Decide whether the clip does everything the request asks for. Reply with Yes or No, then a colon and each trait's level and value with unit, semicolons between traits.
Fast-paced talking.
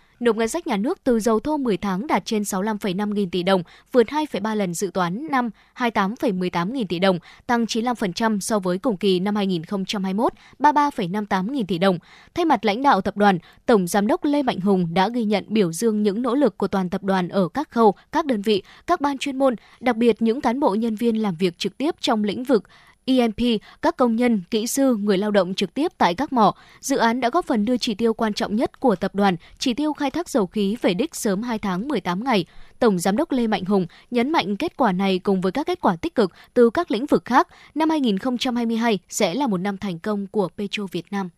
No: average, 235 wpm